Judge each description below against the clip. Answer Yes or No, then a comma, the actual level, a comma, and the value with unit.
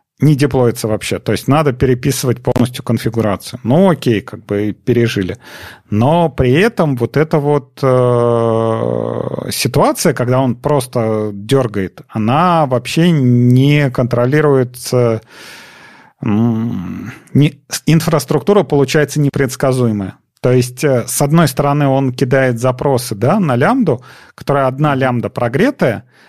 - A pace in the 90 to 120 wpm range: Yes, average, 115 wpm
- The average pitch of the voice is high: No, low, 130 Hz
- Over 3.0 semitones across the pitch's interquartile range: Yes, average, 3.8 semitones